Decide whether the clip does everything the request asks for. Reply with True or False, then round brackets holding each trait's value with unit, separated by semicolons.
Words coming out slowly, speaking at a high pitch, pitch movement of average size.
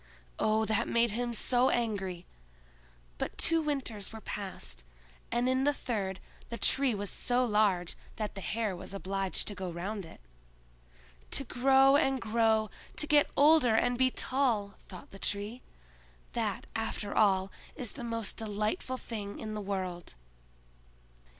False (145 wpm; 215 Hz; 4.1 semitones)